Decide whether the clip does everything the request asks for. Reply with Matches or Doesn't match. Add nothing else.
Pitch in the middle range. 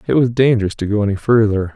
Doesn't match